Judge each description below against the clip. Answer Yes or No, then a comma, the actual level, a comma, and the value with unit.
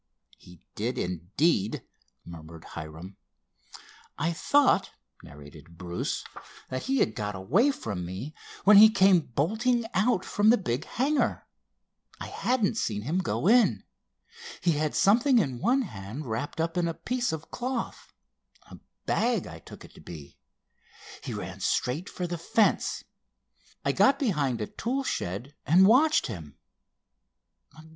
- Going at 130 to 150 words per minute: Yes, average, 140 wpm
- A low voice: No, medium, 160 Hz